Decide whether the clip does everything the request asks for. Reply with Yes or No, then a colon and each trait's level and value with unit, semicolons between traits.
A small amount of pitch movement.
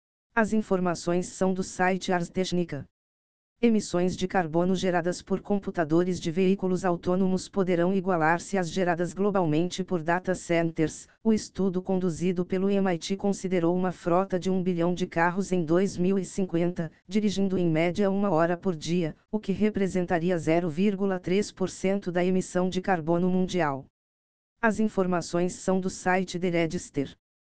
Yes: narrow, 1.8 semitones